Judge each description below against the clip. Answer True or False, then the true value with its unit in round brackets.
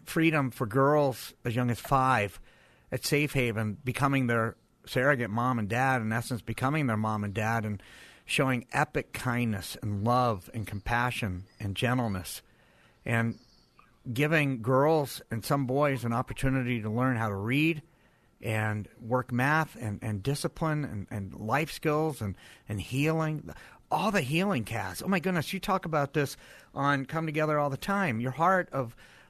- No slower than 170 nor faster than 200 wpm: False (160 wpm)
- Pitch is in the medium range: False (130 Hz)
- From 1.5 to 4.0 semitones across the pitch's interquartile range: False (4.7 semitones)